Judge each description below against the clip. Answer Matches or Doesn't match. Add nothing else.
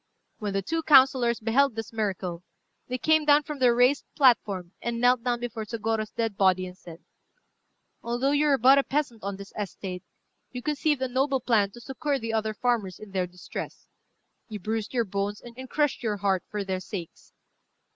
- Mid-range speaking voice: Doesn't match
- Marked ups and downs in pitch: Doesn't match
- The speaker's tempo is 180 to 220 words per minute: Matches